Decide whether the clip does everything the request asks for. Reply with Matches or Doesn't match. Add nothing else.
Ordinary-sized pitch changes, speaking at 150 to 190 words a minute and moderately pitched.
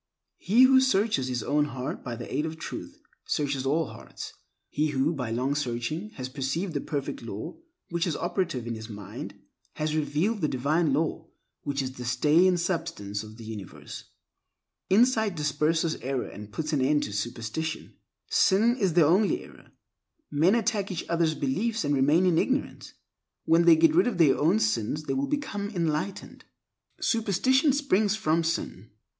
Doesn't match